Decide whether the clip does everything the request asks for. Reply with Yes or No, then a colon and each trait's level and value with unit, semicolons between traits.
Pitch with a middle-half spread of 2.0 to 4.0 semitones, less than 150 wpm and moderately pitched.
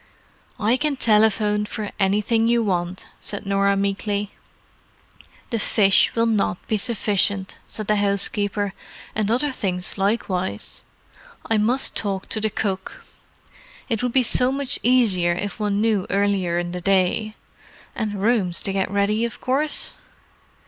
No: narrow, 2.5 semitones; average, 140 wpm; high, 205 Hz